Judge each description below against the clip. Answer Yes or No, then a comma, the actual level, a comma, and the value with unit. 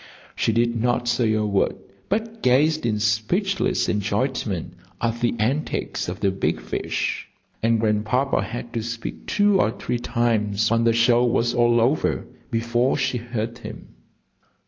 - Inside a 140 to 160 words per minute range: Yes, average, 150 wpm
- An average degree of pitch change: No, narrow, 2.2 semitones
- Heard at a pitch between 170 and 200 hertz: No, low, 120 Hz